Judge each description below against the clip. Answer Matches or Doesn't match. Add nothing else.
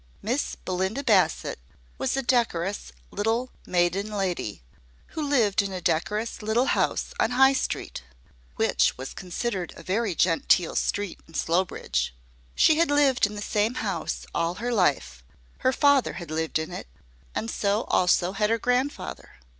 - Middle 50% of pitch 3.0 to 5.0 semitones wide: Doesn't match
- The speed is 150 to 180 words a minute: Matches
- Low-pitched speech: Doesn't match